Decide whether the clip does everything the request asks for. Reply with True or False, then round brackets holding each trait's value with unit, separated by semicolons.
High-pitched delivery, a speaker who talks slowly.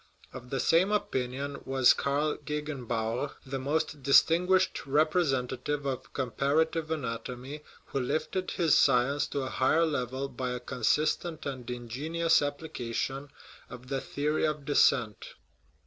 False (140 Hz; 125 wpm)